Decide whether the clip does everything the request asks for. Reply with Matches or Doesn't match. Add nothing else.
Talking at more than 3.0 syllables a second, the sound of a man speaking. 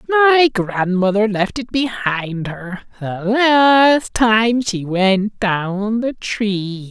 Doesn't match